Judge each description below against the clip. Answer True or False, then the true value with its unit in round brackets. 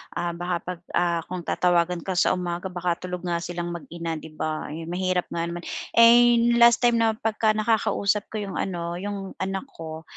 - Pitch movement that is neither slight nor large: True (3.8 semitones)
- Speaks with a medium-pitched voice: True (180 Hz)